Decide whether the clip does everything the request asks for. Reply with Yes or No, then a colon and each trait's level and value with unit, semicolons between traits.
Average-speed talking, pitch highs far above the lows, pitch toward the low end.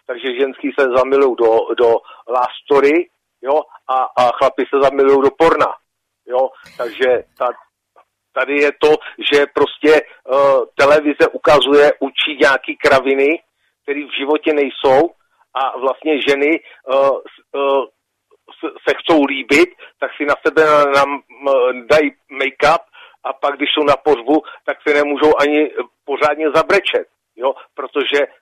No: average, 135 wpm; wide, 6.3 semitones; medium, 150 Hz